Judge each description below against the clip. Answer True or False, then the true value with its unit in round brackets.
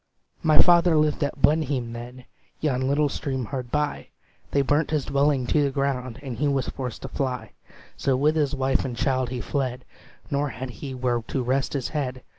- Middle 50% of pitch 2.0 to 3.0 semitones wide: True (2.4 semitones)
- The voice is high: False (135 Hz)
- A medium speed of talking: True (195 wpm)